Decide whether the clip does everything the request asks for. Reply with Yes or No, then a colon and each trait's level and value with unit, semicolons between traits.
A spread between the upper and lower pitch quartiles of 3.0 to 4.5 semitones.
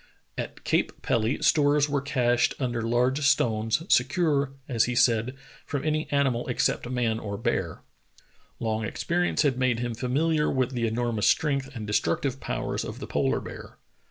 Yes: average, 3.4 semitones